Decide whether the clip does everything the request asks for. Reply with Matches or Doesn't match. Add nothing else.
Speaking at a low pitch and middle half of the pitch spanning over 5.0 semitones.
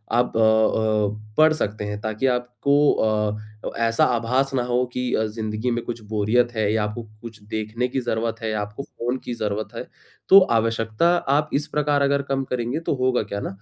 Doesn't match